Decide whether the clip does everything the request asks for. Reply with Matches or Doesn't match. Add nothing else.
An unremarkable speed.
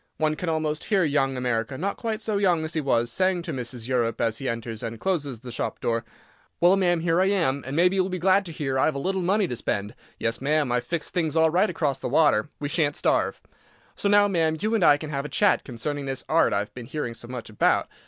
Doesn't match